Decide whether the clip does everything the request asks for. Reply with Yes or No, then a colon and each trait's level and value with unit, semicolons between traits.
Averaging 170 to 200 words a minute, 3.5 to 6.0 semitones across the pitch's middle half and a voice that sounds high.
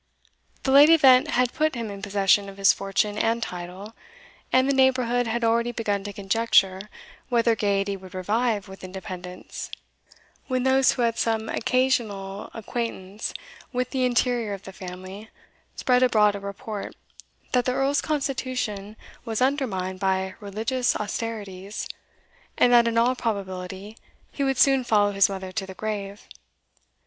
No: average, 150 wpm; average, 4.1 semitones; high, 220 Hz